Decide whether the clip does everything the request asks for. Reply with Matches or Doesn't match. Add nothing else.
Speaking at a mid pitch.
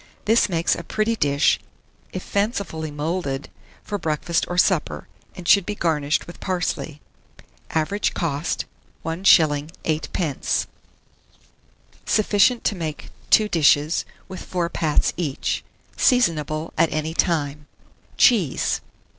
Matches